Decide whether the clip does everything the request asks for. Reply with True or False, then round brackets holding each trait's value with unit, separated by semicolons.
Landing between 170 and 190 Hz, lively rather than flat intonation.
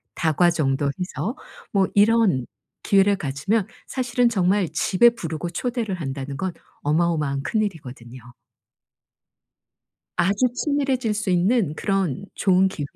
True (185 Hz; 6.1 semitones)